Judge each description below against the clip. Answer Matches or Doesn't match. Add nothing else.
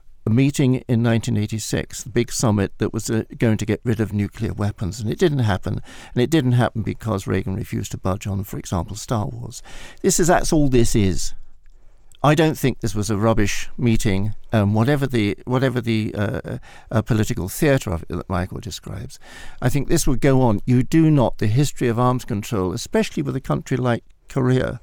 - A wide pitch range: Doesn't match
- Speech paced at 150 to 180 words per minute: Doesn't match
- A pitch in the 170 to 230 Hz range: Doesn't match